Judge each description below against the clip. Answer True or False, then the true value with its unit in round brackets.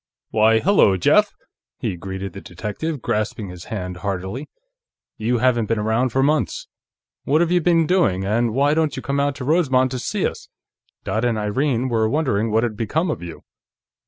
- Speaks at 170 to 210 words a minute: True (185 wpm)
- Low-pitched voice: True (115 Hz)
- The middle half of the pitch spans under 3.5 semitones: False (5.4 semitones)